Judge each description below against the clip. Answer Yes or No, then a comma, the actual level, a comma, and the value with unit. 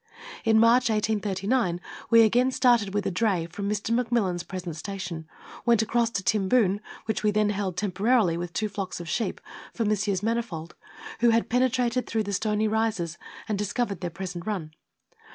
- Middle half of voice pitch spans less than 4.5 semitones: Yes, average, 3.5 semitones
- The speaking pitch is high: Yes, high, 210 Hz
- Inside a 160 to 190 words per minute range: Yes, average, 170 wpm